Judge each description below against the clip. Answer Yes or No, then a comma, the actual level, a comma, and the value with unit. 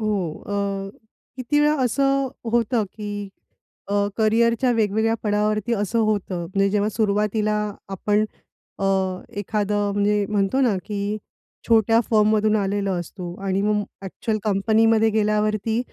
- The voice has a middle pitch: No, high, 210 Hz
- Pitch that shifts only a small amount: Yes, narrow, 1.7 semitones